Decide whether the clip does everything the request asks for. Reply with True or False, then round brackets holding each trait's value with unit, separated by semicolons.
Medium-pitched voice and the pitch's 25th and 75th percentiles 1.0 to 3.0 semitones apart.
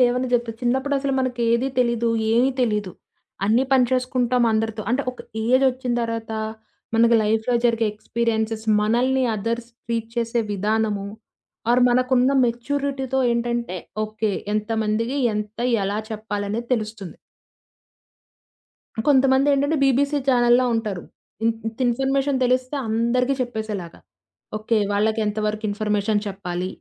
False (235 Hz; 2.7 semitones)